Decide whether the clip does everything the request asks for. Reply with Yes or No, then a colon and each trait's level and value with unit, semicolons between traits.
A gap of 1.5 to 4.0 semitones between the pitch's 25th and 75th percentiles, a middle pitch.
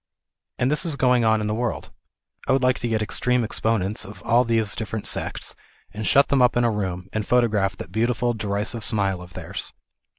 No: average, 2.9 semitones; low, 110 Hz